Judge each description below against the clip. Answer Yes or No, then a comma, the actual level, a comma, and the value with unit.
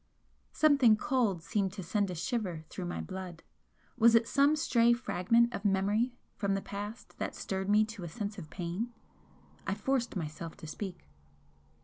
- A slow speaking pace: No, average, 165 wpm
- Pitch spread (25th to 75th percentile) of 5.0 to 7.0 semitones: No, average, 4.2 semitones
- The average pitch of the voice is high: Yes, high, 205 Hz